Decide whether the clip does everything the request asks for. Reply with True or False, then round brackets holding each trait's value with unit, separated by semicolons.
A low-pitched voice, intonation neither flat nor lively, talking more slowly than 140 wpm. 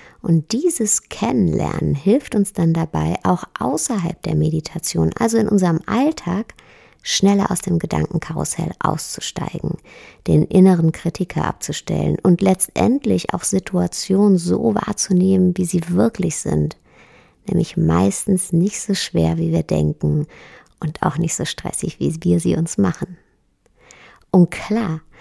False (180 Hz; 3.6 semitones; 130 wpm)